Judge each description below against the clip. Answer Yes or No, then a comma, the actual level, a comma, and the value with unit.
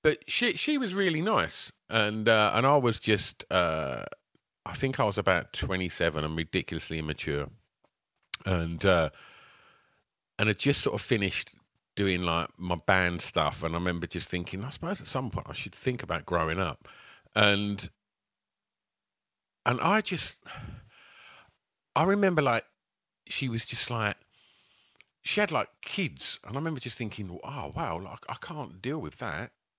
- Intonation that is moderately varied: No, wide, 7.3 semitones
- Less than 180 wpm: Yes, average, 160 wpm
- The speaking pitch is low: Yes, low, 105 Hz